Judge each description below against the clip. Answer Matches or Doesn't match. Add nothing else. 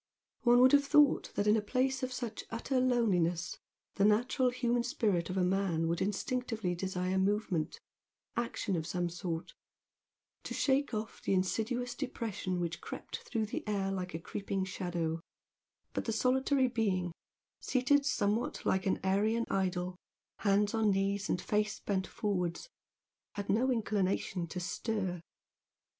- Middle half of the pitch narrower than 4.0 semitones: Doesn't match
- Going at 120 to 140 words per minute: Doesn't match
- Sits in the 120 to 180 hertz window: Doesn't match